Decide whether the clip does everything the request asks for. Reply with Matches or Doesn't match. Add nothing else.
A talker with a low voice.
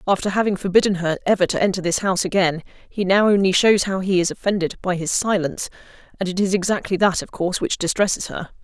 Doesn't match